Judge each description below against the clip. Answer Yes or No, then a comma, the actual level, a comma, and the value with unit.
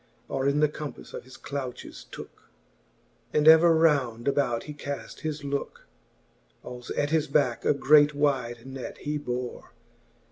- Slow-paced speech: No, average, 150 wpm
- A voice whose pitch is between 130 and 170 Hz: Yes, medium, 140 Hz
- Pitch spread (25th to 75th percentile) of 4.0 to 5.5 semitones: No, average, 2.9 semitones